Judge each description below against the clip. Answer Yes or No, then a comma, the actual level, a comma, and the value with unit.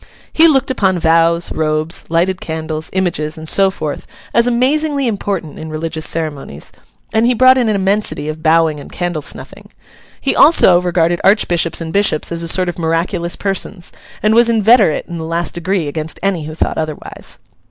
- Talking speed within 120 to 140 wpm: No, average, 175 wpm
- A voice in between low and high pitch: Yes, medium, 170 Hz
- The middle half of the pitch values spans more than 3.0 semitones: Yes, average, 4.2 semitones